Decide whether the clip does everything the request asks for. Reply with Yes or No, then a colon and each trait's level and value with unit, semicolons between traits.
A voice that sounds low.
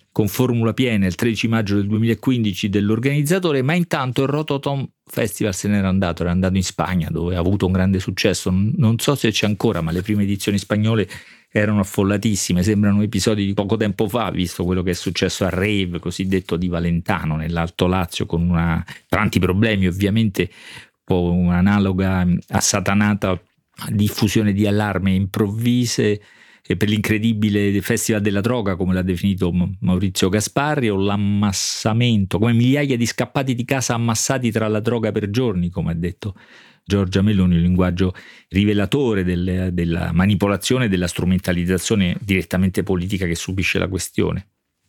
Yes: low, 100 Hz